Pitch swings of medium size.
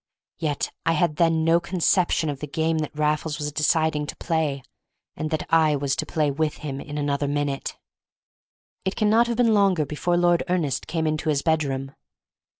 No: narrow, 2.3 semitones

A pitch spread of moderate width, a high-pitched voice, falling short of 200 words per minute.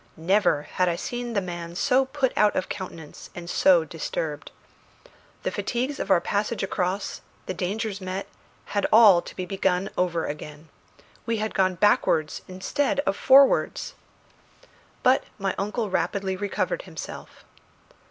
Yes: average, 3.7 semitones; high, 195 Hz; average, 145 wpm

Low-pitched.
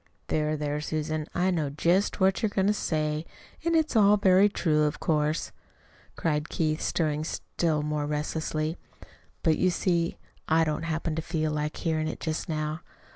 No: medium, 155 Hz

